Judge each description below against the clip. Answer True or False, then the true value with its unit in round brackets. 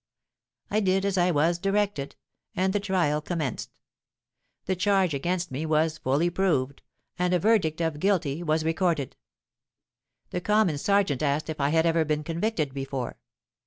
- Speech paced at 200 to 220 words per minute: False (155 wpm)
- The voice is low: False (165 Hz)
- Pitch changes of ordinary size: True (4.0 semitones)